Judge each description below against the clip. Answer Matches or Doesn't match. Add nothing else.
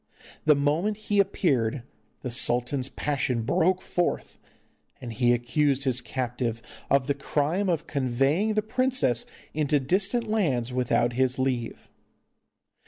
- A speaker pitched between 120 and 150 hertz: Matches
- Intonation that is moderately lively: Doesn't match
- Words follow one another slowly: Matches